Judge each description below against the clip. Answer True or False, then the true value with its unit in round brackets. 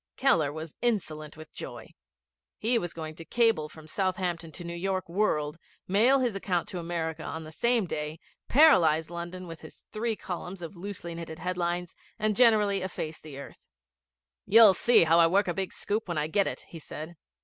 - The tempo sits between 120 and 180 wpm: False (190 wpm)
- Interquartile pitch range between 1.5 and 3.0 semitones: False (4.0 semitones)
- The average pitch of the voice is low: False (175 Hz)